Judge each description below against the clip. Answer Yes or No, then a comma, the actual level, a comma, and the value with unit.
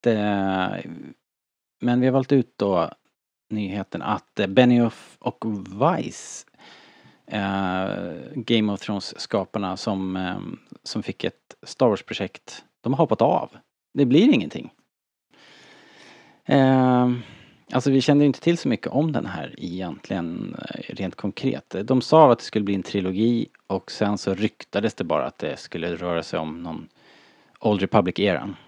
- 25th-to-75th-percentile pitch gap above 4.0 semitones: Yes, average, 4.5 semitones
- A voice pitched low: Yes, low, 105 Hz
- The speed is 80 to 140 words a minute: Yes, average, 130 wpm